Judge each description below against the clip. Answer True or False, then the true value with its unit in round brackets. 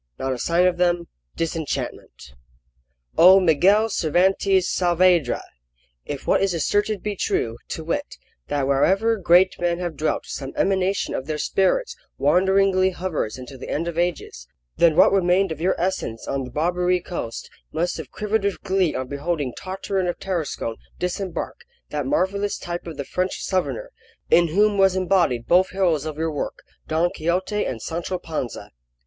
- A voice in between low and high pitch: True (175 Hz)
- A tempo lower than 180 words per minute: True (160 wpm)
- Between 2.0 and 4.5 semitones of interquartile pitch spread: True (3.5 semitones)